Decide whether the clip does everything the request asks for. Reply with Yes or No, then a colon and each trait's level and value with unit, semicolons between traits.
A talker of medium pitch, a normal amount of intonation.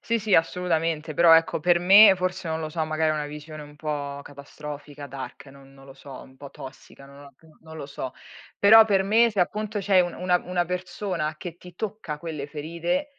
Yes: medium, 160 Hz; average, 3.7 semitones